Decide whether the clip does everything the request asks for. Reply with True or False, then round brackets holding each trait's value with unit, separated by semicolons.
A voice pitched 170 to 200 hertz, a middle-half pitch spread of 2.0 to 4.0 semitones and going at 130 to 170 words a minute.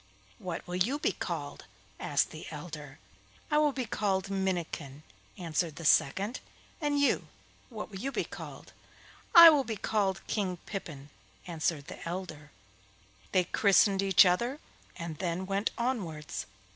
False (190 Hz; 4.7 semitones; 145 wpm)